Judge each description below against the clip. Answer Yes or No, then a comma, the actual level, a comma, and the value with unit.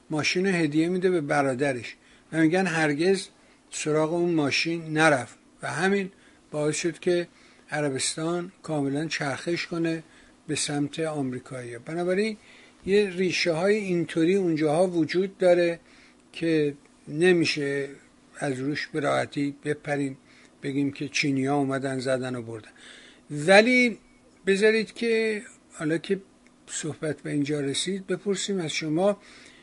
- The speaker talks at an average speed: Yes, average, 115 wpm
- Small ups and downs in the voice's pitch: No, average, 4.3 semitones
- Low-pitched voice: No, medium, 160 Hz